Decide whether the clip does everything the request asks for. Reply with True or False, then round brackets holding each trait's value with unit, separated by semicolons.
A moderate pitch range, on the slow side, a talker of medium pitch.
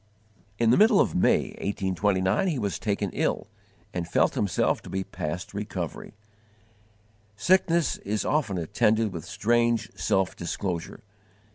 False (4.0 semitones; 130 wpm; 100 Hz)